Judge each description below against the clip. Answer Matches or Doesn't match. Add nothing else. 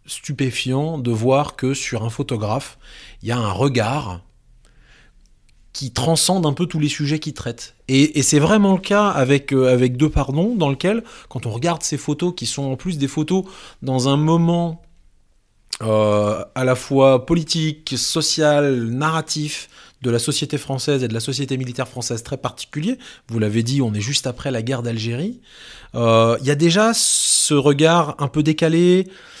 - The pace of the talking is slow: Doesn't match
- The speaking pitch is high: Doesn't match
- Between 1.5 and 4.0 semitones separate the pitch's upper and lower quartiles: Doesn't match